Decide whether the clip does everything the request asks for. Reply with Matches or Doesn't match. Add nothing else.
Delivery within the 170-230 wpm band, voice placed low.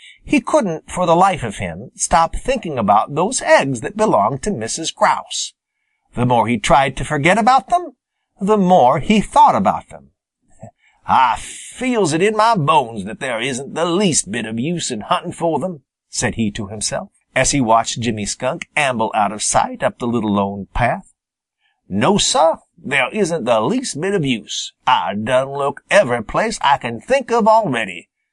Doesn't match